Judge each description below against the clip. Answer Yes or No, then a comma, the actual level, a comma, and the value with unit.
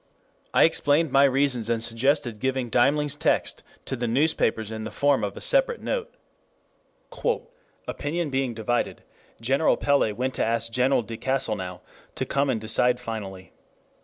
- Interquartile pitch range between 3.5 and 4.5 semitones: Yes, average, 3.9 semitones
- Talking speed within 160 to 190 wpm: No, average, 150 wpm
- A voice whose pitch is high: No, low, 125 Hz